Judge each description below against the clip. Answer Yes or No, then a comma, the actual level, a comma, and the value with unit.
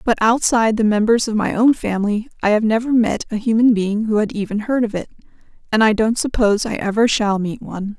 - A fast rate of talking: Yes, fast, 225 wpm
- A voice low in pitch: No, high, 220 Hz